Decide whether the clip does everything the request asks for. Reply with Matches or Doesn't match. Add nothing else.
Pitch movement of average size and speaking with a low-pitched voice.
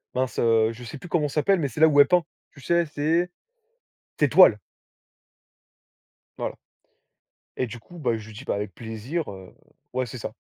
Doesn't match